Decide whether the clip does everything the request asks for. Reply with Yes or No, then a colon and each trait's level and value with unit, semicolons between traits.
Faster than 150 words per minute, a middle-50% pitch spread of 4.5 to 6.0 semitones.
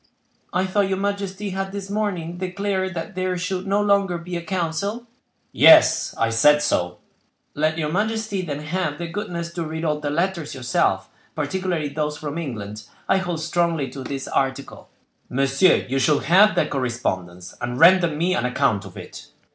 Yes: average, 170 wpm; average, 4.8 semitones